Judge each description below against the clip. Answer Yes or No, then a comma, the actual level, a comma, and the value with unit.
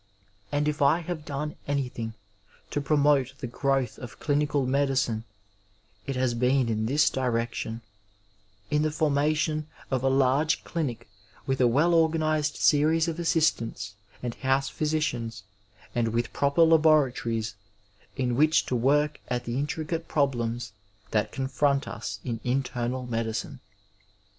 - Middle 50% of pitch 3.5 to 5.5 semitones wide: Yes, average, 3.9 semitones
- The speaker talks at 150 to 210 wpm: No, slow, 135 wpm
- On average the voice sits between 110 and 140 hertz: Yes, low, 135 Hz